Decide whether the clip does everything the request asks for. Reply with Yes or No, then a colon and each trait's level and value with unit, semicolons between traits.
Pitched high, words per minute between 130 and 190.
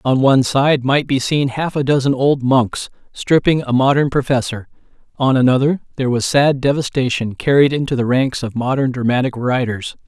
No: low, 130 Hz; average, 175 wpm